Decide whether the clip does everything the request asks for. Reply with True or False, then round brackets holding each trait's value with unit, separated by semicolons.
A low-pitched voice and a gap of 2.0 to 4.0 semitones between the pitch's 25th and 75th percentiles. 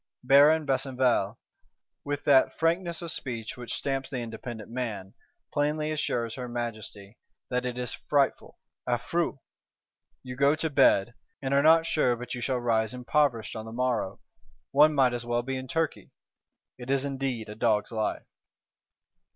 True (125 Hz; 3.2 semitones)